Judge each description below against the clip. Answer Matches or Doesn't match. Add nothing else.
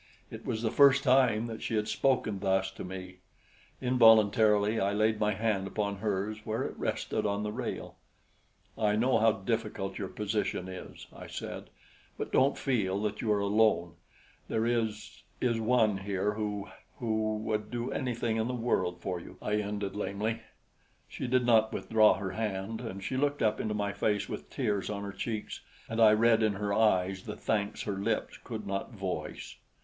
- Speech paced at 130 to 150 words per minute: Doesn't match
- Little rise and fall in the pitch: Matches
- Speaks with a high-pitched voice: Doesn't match